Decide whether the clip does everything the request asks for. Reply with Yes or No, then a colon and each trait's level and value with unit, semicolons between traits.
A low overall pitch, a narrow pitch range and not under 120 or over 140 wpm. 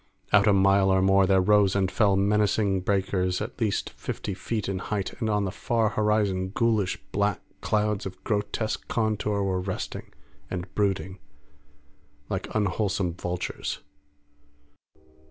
Yes: low, 100 Hz; narrow, 1.9 semitones; slow, 135 wpm